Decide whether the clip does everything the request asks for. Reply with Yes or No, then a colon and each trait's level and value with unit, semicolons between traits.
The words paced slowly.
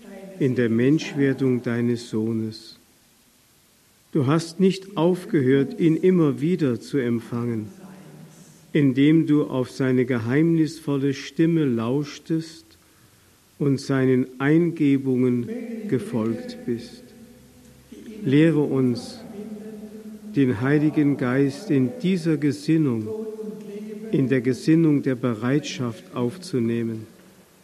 Yes: slow, 85 wpm